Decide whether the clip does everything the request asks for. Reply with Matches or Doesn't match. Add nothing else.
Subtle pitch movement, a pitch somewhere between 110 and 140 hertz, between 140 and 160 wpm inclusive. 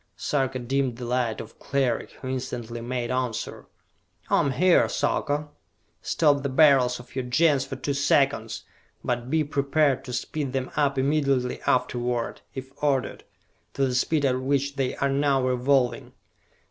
Matches